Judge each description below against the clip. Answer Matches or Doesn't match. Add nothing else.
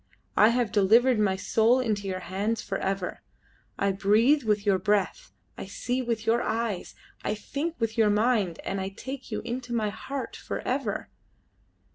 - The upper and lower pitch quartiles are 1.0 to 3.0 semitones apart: Doesn't match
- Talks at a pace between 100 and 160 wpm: Doesn't match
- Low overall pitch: Doesn't match